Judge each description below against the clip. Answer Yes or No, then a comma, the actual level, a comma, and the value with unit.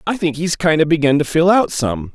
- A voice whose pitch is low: No, medium, 155 Hz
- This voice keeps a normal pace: No, fast, 280 wpm